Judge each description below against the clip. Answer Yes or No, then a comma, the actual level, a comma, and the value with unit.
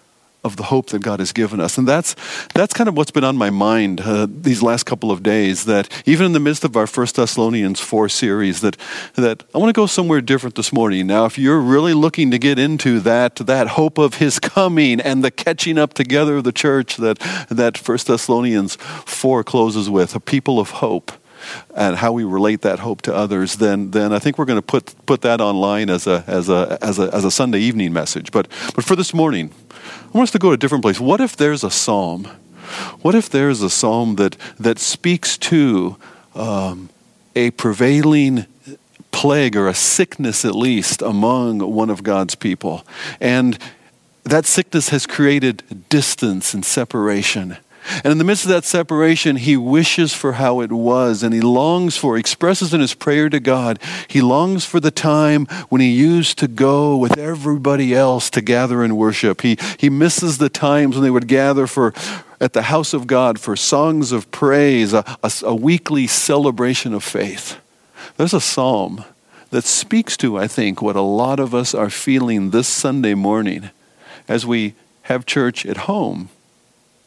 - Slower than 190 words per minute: No, average, 195 wpm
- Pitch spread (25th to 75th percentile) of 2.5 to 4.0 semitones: No, average, 5.1 semitones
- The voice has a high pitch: No, low, 130 Hz